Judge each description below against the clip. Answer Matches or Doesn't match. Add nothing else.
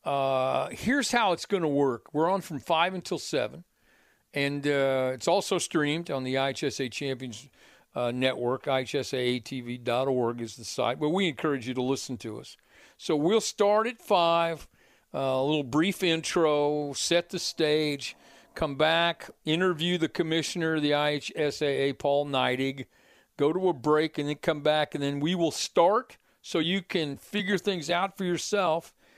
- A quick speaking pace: Doesn't match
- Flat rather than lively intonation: Doesn't match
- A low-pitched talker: Doesn't match